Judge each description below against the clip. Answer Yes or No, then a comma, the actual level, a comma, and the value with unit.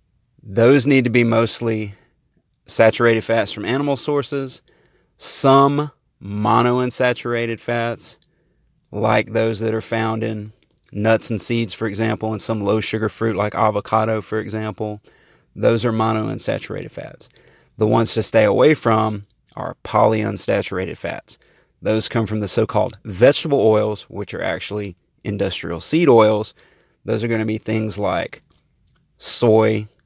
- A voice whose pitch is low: Yes, low, 110 Hz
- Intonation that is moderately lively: No, narrow, 1.5 semitones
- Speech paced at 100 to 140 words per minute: Yes, slow, 135 wpm